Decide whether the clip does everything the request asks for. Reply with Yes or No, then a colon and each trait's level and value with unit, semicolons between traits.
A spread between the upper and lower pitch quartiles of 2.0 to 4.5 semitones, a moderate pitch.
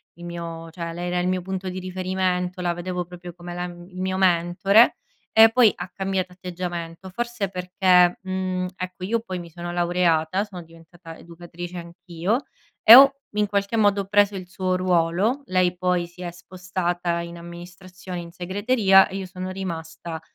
No: narrow, 1.5 semitones; medium, 180 Hz